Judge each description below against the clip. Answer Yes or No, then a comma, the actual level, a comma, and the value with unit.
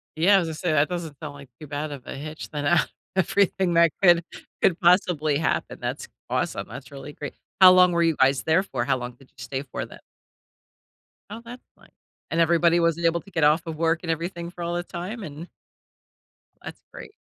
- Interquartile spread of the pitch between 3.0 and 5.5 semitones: No, narrow, 2.6 semitones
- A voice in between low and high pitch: Yes, medium, 165 Hz